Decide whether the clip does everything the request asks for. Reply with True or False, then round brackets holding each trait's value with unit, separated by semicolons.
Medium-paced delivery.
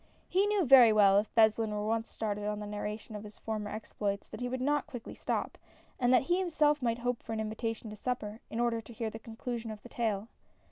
False (235 wpm)